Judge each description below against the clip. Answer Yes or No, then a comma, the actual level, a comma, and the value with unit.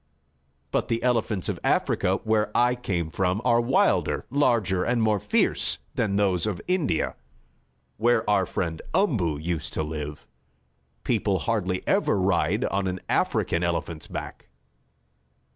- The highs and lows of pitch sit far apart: No, average, 4.9 semitones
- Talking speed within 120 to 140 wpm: Yes, slow, 135 wpm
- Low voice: Yes, low, 100 Hz